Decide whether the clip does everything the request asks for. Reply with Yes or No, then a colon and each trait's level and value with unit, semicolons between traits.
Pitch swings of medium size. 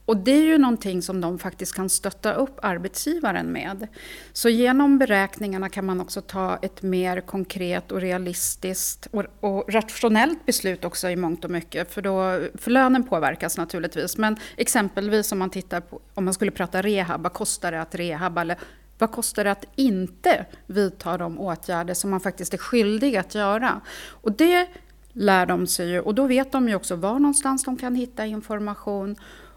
Yes: average, 3.7 semitones